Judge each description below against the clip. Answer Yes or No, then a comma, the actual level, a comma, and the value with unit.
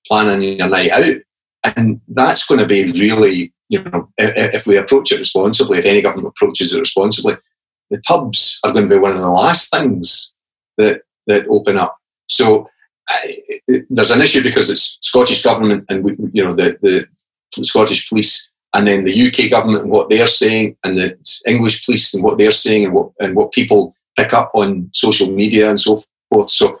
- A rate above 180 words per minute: Yes, average, 190 wpm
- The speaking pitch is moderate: No, low, 110 Hz